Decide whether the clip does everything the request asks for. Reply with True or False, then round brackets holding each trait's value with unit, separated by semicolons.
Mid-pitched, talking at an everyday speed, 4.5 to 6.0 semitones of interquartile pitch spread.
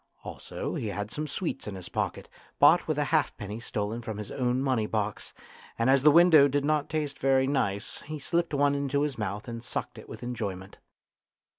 False (130 Hz; 195 wpm; 5.2 semitones)